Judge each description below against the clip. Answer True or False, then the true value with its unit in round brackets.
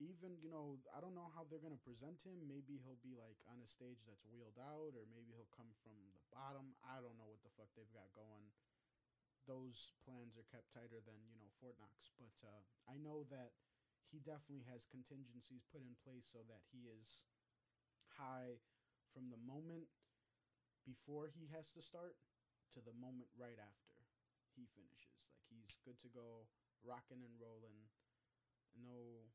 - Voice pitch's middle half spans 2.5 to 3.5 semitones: True (2.9 semitones)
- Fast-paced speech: False (180 wpm)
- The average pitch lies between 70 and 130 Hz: True (125 Hz)